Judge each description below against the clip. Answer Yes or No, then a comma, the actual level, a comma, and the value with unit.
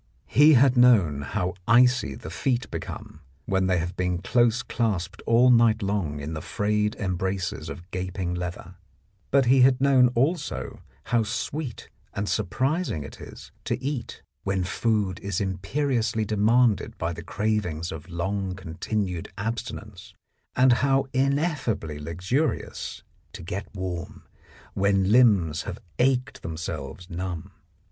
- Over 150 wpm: No, slow, 135 wpm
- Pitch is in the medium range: No, low, 100 Hz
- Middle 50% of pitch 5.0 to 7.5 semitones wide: Yes, wide, 5.6 semitones